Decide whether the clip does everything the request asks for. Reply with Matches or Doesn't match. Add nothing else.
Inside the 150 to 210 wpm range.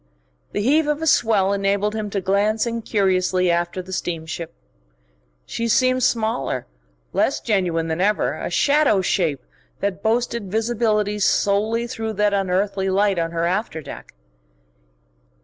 Doesn't match